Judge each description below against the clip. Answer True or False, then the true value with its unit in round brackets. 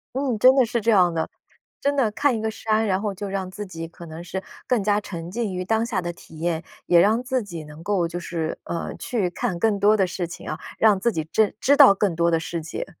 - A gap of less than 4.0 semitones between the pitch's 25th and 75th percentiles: False (4.4 semitones)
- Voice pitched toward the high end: True (195 Hz)